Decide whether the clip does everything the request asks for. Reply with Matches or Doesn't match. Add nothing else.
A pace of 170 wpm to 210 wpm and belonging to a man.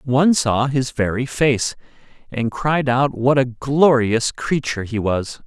Doesn't match